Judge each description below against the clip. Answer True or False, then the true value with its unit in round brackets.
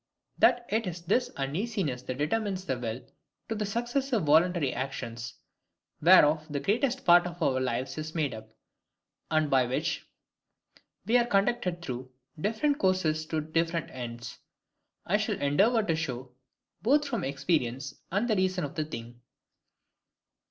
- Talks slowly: False (145 wpm)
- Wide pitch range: True (7.2 semitones)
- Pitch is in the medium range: True (160 Hz)